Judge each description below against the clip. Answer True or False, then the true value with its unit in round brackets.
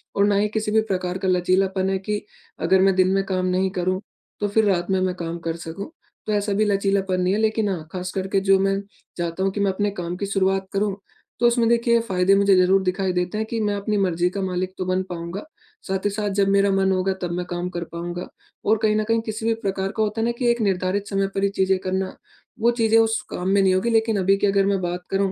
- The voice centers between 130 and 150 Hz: False (195 Hz)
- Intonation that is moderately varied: False (1.9 semitones)